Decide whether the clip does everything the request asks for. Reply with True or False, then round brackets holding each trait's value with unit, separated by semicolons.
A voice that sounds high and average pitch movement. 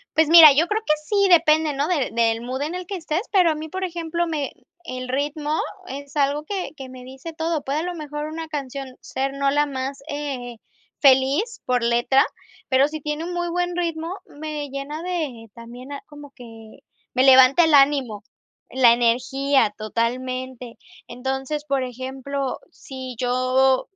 True (280 Hz; 3.5 semitones)